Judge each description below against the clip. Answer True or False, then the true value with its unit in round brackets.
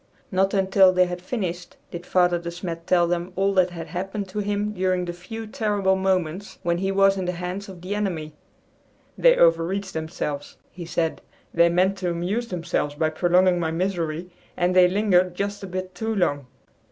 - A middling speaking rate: True (190 wpm)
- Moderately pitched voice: True (180 Hz)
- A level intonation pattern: True (2.2 semitones)